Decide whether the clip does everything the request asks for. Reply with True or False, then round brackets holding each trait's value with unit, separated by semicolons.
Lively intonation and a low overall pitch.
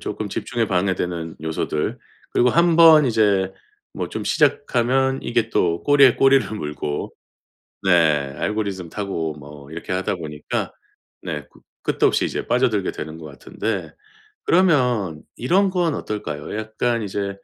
True (7.1 semitones; 105 Hz)